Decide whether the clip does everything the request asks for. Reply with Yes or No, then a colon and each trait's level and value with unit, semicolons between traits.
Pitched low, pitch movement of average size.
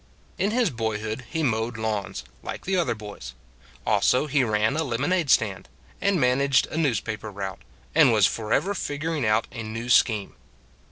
No: low, 115 Hz; wide, 5.7 semitones